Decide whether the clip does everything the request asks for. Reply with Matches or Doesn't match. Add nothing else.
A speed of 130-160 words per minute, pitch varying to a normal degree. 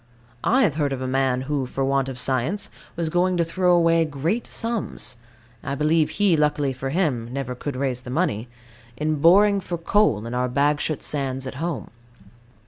Doesn't match